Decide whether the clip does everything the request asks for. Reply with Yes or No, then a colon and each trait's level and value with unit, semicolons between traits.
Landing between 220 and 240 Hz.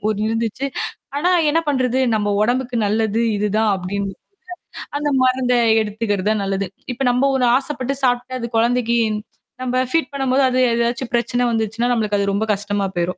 Yes: high, 235 Hz